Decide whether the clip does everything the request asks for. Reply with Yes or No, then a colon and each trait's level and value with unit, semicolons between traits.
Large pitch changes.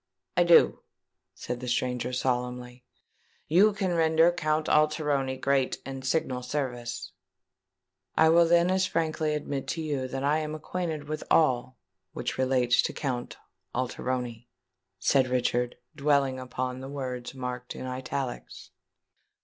No: average, 3.5 semitones